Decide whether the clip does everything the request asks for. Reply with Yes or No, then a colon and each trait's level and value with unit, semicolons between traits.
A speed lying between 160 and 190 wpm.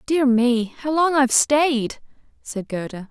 Yes: average, 175 wpm